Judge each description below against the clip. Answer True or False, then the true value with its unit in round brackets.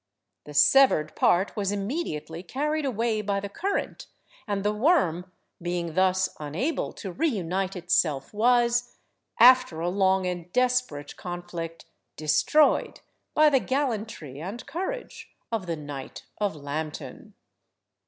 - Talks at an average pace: False (125 wpm)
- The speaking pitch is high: True (195 Hz)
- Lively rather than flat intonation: True (6.7 semitones)